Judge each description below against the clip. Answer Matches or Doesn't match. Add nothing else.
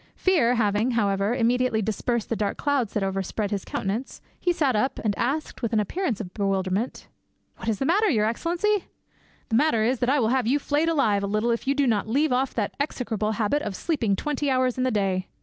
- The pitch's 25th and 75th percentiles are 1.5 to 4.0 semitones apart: Doesn't match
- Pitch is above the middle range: Matches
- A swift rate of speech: Matches